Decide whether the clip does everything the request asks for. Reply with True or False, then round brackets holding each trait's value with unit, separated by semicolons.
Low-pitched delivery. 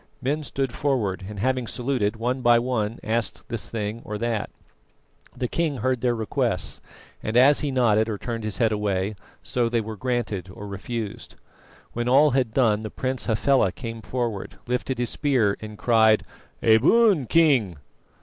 True (115 Hz)